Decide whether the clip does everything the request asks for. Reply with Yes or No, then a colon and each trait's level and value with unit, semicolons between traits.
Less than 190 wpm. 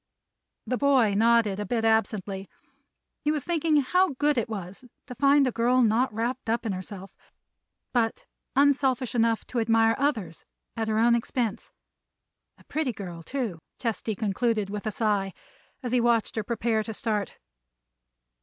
Yes: average, 155 wpm